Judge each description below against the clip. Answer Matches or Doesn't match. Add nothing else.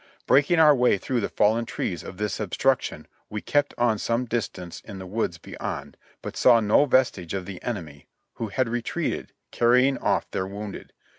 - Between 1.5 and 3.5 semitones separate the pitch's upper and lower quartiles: Doesn't match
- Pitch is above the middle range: Doesn't match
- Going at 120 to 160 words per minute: Doesn't match